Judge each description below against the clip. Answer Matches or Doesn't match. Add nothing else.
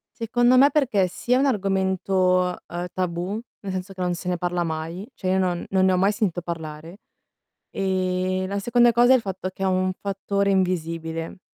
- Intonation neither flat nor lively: Doesn't match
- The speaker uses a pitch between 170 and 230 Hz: Matches